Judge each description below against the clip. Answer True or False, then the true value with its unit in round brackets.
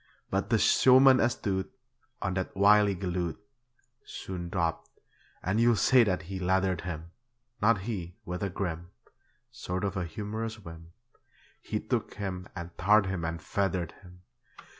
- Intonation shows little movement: False (3.0 semitones)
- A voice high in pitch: False (95 Hz)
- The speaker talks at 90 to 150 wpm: True (140 wpm)